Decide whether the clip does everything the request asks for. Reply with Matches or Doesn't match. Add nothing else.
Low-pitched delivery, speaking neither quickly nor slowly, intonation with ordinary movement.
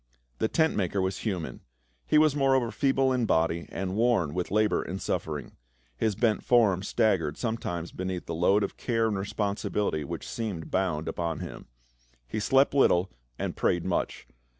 Matches